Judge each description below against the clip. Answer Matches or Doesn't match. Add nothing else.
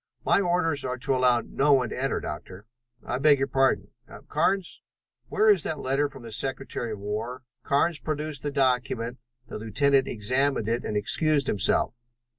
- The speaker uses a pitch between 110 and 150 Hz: Matches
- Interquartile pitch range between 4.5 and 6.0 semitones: Doesn't match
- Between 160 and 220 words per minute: Matches